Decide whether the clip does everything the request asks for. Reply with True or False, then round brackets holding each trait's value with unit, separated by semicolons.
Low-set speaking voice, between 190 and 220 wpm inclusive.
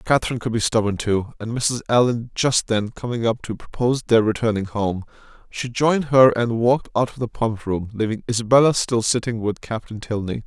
True (115 Hz; 200 wpm)